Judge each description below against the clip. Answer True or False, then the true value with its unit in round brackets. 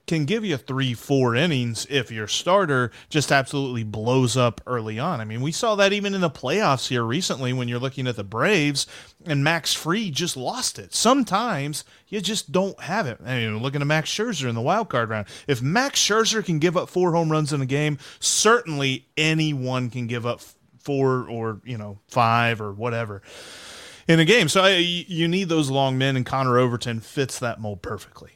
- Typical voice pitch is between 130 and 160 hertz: True (140 Hz)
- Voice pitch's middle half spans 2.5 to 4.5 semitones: False (5.6 semitones)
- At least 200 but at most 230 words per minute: True (205 wpm)